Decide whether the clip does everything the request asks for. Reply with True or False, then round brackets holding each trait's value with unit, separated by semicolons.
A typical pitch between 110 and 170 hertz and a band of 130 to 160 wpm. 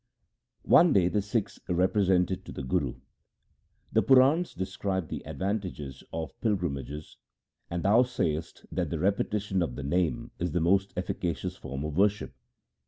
False (95 Hz; 150 wpm)